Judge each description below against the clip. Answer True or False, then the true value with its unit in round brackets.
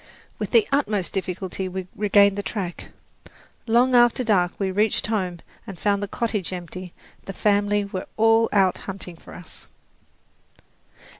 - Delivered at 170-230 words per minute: False (145 wpm)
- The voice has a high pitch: True (200 Hz)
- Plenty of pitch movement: False (2.8 semitones)